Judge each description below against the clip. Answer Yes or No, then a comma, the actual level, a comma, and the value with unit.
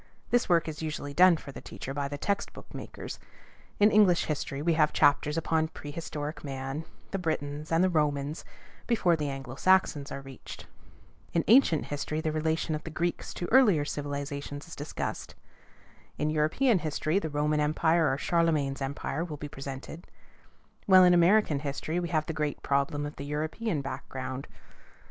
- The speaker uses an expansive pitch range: No, average, 2.8 semitones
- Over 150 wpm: Yes, average, 170 wpm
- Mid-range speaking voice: Yes, medium, 155 Hz